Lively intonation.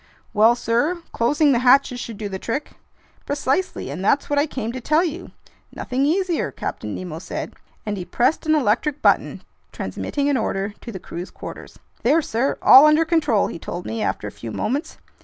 Yes: wide, 5.9 semitones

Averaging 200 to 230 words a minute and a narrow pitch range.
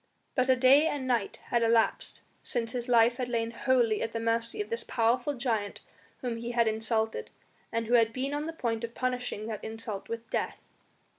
Yes: fast, 205 wpm; narrow, 2.0 semitones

